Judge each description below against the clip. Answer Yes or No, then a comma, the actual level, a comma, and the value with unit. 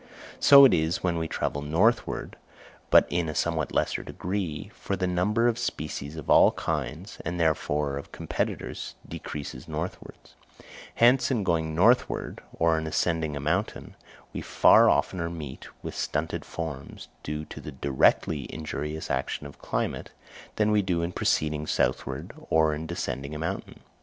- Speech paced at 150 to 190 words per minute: Yes, average, 155 wpm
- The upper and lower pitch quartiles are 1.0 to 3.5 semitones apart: Yes, average, 2.9 semitones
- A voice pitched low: Yes, very low, 80 Hz